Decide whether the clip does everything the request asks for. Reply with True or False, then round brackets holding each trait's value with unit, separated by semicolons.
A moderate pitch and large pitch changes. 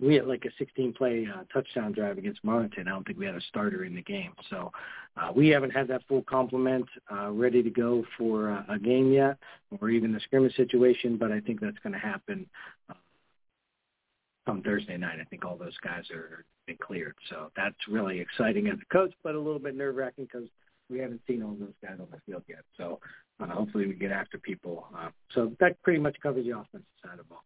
False (130 Hz; 6.8 semitones)